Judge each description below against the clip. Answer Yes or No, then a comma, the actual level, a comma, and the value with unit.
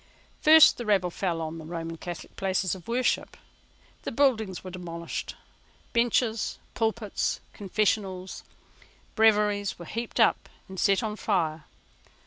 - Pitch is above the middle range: Yes, high, 195 Hz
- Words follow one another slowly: Yes, slow, 125 wpm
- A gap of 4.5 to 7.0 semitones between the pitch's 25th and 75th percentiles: No, average, 4.0 semitones